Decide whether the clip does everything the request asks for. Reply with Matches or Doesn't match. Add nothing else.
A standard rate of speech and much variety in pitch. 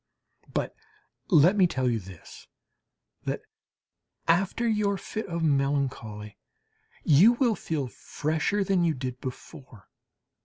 Doesn't match